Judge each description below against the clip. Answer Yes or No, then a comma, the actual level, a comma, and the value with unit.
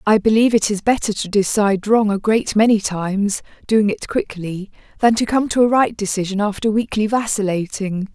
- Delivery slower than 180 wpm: Yes, average, 170 wpm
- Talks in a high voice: Yes, high, 210 Hz